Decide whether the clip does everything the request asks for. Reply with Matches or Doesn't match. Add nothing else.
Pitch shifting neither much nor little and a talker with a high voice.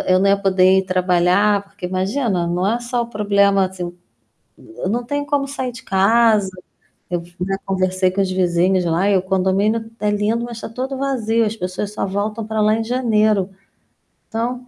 Matches